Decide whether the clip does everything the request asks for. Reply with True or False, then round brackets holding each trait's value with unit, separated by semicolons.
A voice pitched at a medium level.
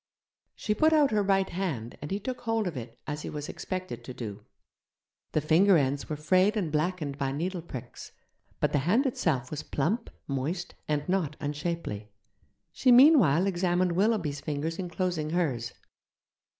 True (170 Hz)